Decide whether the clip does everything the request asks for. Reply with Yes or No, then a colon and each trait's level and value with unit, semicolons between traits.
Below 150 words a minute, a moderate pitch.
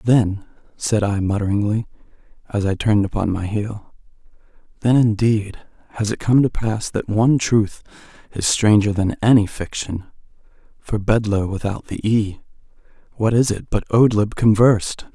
No: average, 140 wpm; low, 105 Hz